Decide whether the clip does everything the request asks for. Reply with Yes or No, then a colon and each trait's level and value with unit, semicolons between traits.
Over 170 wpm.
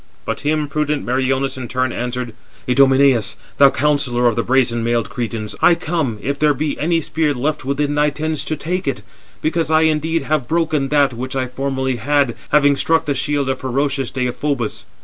Yes: average, 185 wpm